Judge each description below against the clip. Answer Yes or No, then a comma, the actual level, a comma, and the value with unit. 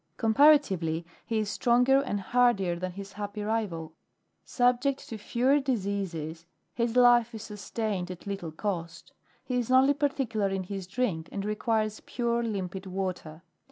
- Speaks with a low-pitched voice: No, high, 210 Hz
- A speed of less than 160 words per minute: Yes, average, 145 wpm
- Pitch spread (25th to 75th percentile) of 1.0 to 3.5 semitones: No, average, 4.5 semitones